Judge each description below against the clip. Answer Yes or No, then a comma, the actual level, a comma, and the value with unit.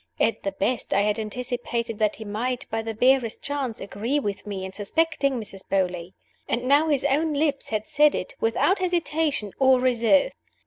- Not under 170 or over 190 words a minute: Yes, average, 180 wpm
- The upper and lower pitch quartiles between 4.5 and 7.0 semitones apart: Yes, average, 5.1 semitones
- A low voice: No, high, 240 Hz